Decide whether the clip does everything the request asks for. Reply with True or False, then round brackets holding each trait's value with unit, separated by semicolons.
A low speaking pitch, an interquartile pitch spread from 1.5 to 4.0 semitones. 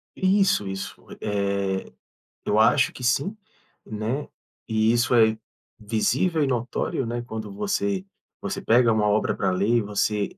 False (110 Hz; 4.5 semitones)